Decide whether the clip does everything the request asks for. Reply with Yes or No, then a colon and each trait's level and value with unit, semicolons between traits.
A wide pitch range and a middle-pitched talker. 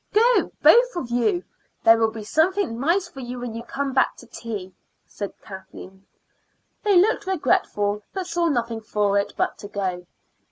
No: wide, 9.0 semitones; high, 240 Hz